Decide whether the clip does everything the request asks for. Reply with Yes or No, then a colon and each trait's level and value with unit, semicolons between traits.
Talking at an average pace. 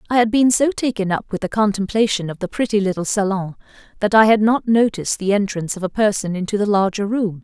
No: fast, 225 wpm